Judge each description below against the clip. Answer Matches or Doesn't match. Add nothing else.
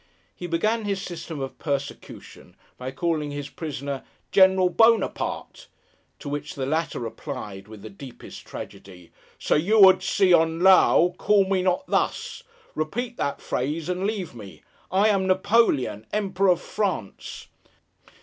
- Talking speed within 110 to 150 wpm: Matches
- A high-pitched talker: Doesn't match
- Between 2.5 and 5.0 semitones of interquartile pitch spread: Doesn't match